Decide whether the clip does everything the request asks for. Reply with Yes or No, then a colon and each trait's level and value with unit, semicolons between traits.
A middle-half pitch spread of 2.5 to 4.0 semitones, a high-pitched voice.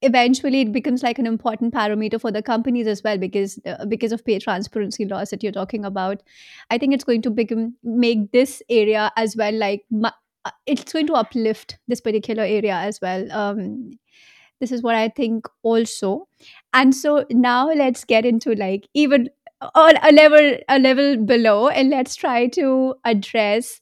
Yes: average, 3.4 semitones; high, 235 Hz